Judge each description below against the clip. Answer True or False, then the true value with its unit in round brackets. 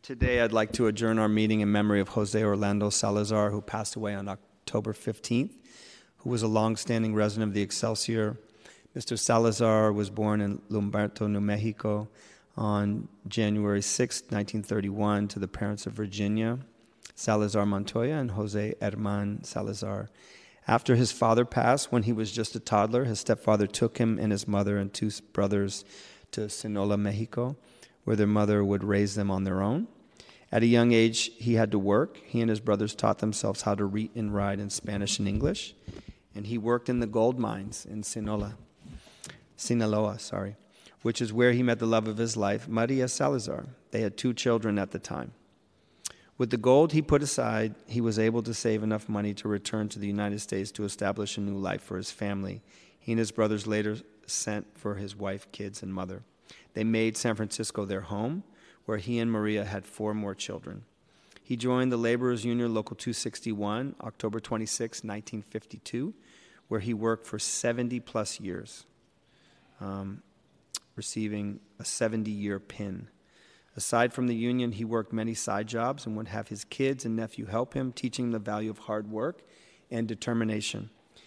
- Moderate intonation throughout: False (2.0 semitones)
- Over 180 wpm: False (175 wpm)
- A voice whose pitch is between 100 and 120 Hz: True (110 Hz)